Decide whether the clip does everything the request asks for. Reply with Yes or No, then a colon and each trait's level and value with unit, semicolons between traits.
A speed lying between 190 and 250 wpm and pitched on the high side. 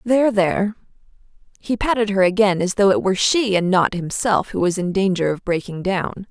Yes: average, 200 wpm; high, 195 Hz